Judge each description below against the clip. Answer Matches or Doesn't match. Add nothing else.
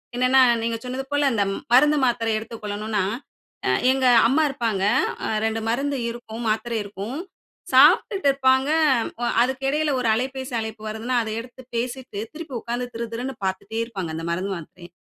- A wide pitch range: Doesn't match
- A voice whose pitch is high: Matches